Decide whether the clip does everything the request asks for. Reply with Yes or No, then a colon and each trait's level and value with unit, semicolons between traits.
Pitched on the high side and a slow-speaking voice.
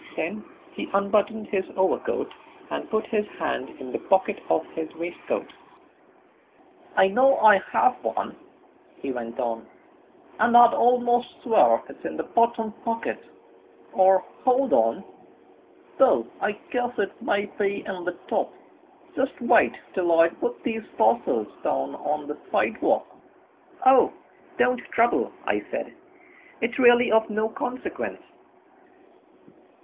Yes: high, 210 Hz; slow, 130 wpm